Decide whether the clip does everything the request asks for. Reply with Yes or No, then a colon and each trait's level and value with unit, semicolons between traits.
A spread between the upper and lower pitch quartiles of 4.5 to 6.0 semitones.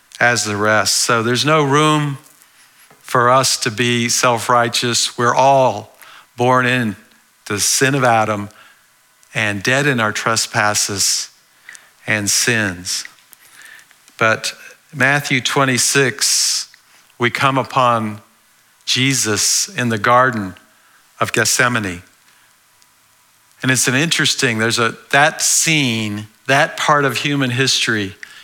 No: average, 3.6 semitones